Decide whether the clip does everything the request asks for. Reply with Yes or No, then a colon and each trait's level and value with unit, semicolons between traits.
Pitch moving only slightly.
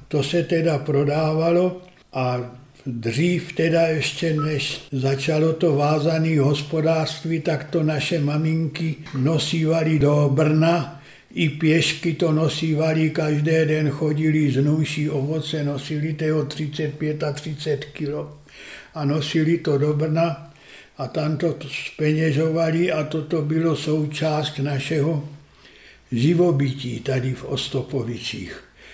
Yes: narrow, 1.9 semitones